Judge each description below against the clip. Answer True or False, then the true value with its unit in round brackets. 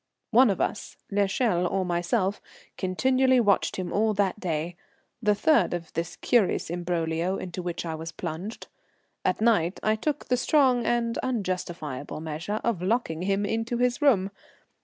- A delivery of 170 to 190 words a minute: False (155 wpm)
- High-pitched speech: True (195 Hz)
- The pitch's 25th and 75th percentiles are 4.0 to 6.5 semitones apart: True (5.2 semitones)